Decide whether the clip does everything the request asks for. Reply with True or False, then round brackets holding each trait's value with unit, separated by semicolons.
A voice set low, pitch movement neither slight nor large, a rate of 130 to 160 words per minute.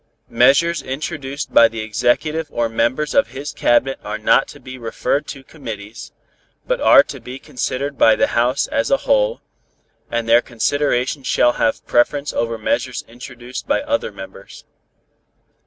True (130 Hz; 4.0 semitones; 155 wpm)